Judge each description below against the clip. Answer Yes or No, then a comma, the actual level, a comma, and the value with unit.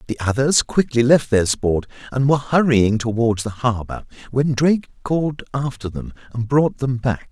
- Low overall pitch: Yes, low, 125 Hz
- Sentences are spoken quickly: No, average, 170 wpm